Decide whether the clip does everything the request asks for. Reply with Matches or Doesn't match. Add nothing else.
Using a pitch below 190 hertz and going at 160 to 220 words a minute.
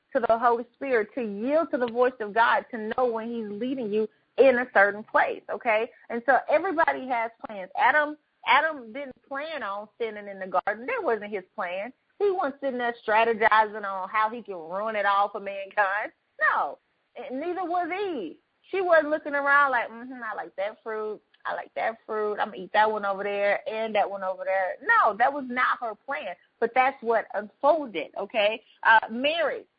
Doesn't match